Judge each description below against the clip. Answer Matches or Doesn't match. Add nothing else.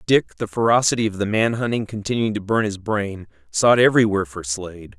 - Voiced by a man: Matches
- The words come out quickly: Doesn't match